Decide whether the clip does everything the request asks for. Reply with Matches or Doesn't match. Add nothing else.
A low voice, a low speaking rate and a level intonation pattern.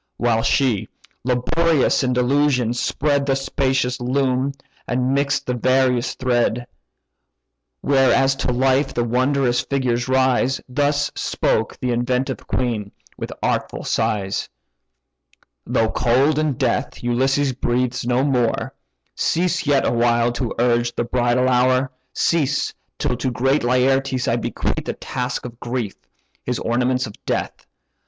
Matches